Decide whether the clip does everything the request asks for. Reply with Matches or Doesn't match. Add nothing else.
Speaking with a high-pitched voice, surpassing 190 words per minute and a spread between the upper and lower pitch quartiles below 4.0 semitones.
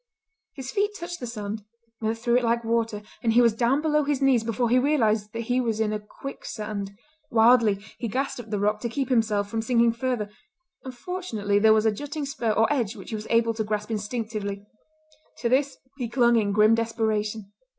Matches